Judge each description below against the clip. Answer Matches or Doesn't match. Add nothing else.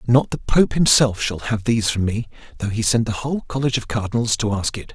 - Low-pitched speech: Matches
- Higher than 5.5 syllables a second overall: Matches